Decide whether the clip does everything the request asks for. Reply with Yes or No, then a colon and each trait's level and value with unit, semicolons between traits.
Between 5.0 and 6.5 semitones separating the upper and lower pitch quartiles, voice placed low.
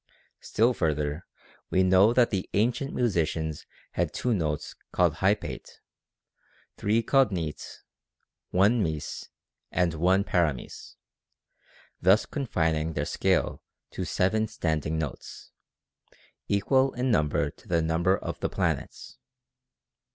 Yes: average, 5.3 semitones; very low, 95 Hz